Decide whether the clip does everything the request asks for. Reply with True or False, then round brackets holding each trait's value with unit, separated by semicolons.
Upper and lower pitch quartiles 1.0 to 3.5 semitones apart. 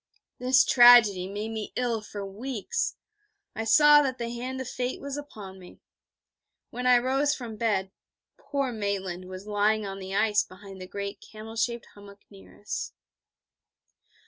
False (3.9 semitones)